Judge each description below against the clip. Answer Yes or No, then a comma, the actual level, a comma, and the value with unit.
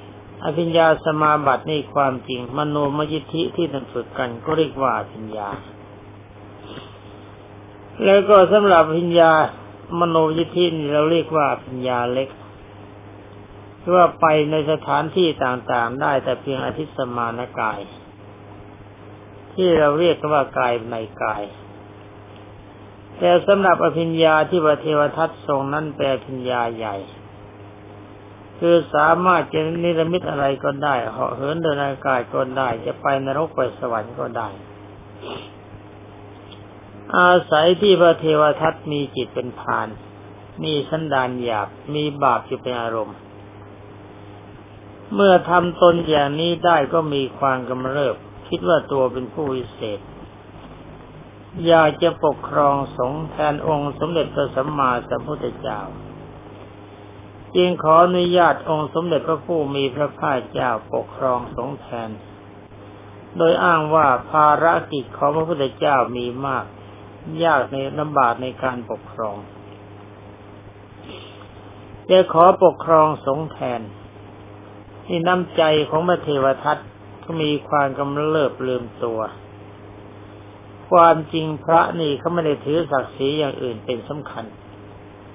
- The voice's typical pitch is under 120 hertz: No, low, 130 Hz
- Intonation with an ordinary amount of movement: No, wide, 7.2 semitones